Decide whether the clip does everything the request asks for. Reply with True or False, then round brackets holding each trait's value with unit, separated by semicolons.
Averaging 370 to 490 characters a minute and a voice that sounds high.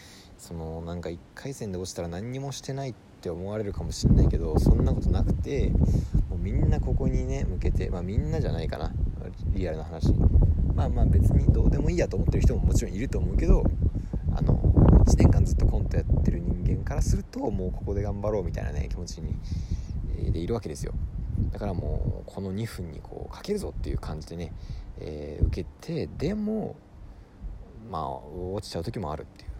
False (385 characters per minute; 90 Hz)